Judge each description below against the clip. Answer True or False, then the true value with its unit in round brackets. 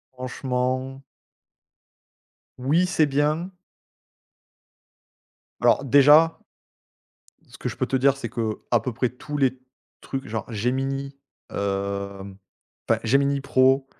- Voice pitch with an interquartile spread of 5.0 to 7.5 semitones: False (2.9 semitones)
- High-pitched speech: False (130 Hz)